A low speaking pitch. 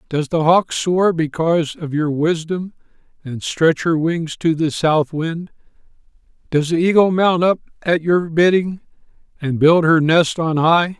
No: medium, 165 Hz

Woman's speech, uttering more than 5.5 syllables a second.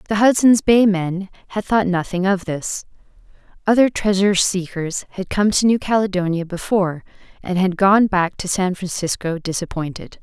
No: female; 5.0 syllables/s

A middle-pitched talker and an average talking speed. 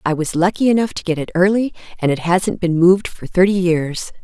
No: medium, 180 Hz; fast, 225 wpm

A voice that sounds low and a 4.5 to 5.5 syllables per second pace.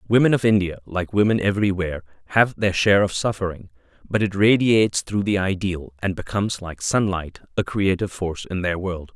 No: very low, 95 Hz; 5.7 syllables/s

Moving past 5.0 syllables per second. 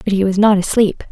Yes: 6.0 syllables/s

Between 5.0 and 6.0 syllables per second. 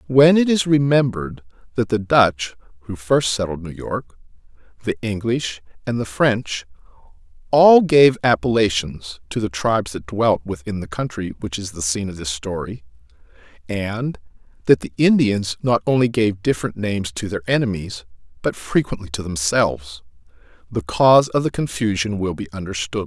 No: 4.8 syllables/s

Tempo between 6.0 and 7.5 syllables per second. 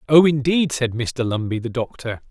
No: 4.9 syllables/s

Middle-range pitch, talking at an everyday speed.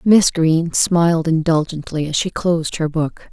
Yes: medium, 165 Hz; average, 165 wpm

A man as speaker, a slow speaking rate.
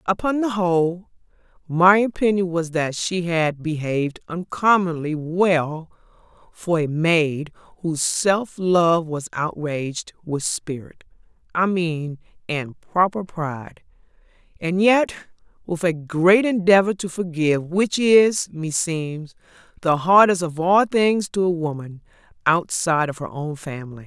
No: female; slow, 125 wpm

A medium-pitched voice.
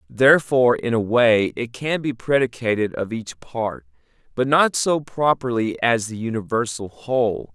No: low, 120 Hz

